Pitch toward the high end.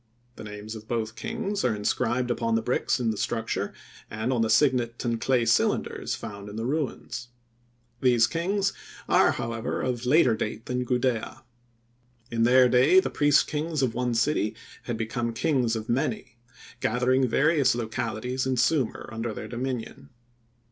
No: low, 120 Hz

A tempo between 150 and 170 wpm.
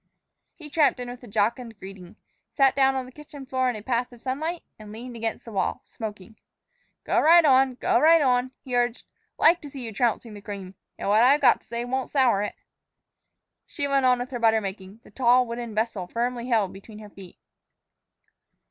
No: fast, 205 wpm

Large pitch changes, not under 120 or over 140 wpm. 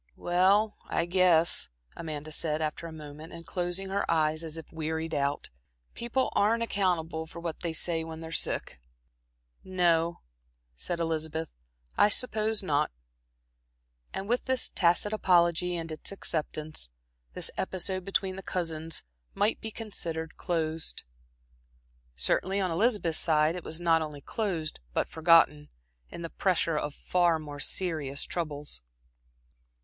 No: average, 2.9 semitones; slow, 135 wpm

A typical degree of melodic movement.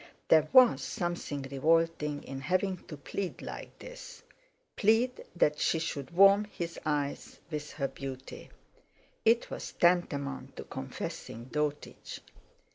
Yes: average, 4.6 semitones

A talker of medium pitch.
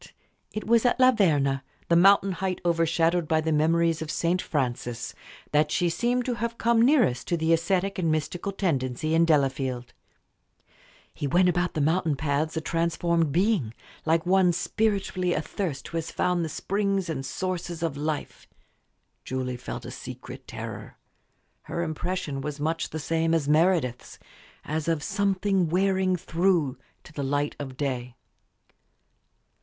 Yes: medium, 165 Hz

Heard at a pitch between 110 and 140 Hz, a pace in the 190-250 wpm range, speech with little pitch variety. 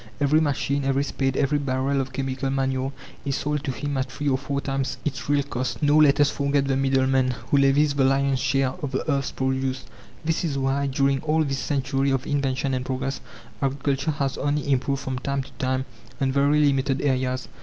Yes: low, 135 Hz; average, 200 wpm; narrow, 1.2 semitones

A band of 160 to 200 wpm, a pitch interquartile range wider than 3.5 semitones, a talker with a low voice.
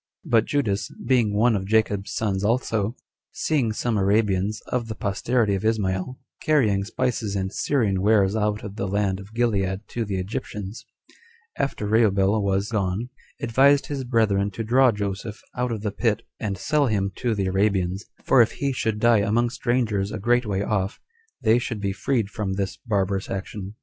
No: average, 175 wpm; average, 3.1 semitones; low, 105 Hz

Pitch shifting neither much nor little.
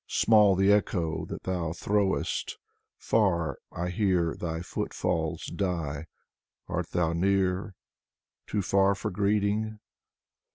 Yes: average, 3.2 semitones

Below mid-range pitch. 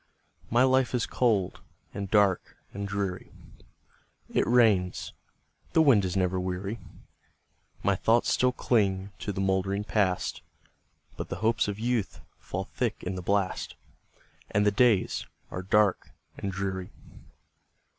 Yes: low, 100 Hz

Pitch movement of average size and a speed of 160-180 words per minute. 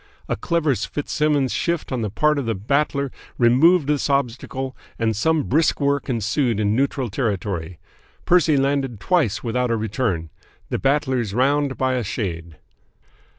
No: average, 4.4 semitones; average, 150 wpm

